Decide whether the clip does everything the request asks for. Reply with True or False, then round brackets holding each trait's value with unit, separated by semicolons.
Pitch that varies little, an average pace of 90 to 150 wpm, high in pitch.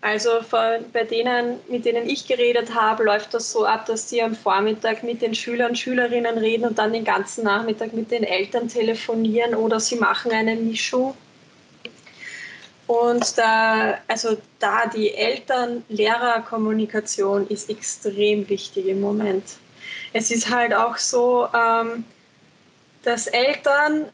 True (1.7 semitones; 140 wpm; 230 Hz)